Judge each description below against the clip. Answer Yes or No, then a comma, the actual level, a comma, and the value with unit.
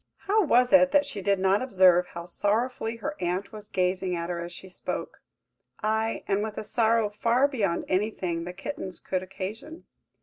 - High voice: Yes, high, 205 Hz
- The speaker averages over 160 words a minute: Yes, average, 180 wpm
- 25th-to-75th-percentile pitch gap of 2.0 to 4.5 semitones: Yes, average, 4.0 semitones